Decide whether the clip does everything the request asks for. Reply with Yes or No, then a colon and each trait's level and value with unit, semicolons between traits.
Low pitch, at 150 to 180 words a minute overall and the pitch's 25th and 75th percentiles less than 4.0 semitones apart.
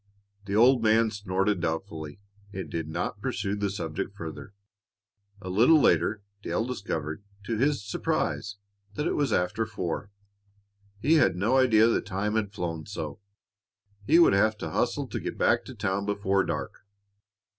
Yes: low, 100 Hz; average, 155 wpm; average, 3.2 semitones